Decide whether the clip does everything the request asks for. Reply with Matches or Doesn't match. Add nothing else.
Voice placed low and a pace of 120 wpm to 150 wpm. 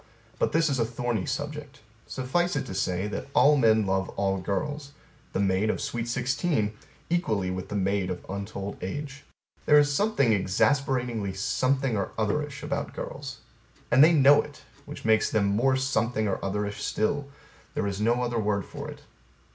Doesn't match